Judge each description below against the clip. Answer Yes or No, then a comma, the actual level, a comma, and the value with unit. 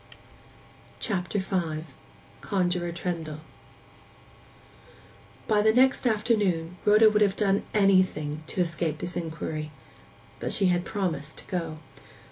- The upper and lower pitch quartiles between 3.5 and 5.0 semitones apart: Yes, average, 4.0 semitones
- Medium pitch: Yes, medium, 180 Hz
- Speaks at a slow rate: Yes, slow, 105 wpm